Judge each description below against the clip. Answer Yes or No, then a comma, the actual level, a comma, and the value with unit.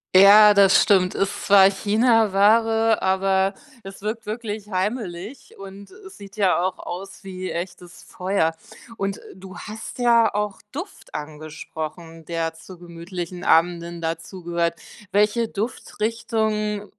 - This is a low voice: No, high, 195 Hz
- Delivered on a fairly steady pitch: No, average, 3.3 semitones